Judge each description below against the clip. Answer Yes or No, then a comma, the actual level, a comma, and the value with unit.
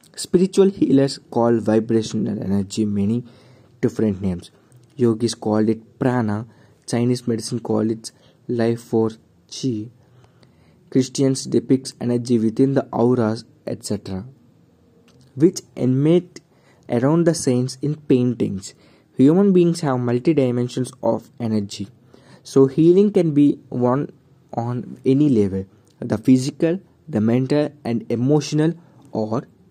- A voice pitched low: Yes, low, 125 Hz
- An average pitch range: Yes, average, 3.6 semitones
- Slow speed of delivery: Yes, slow, 110 wpm